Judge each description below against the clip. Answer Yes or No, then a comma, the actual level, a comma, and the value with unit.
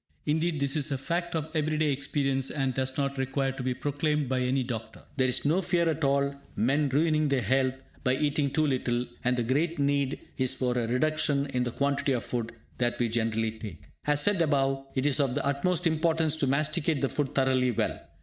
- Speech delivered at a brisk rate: Yes, fast, 215 wpm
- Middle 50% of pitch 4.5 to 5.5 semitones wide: No, average, 2.9 semitones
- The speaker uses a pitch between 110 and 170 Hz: Yes, medium, 140 Hz